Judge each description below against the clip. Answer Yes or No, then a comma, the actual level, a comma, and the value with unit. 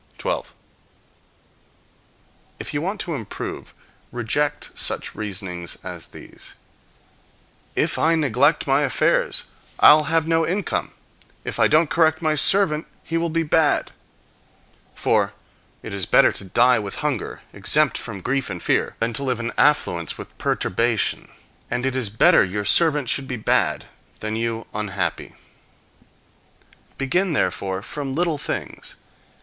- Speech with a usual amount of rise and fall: No, wide, 6.3 semitones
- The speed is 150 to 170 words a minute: No, slow, 135 wpm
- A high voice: No, low, 135 Hz